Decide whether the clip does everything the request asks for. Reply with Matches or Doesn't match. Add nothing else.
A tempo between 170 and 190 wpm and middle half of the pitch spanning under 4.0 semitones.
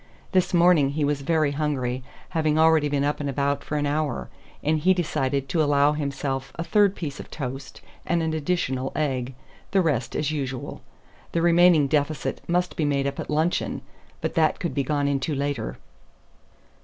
Matches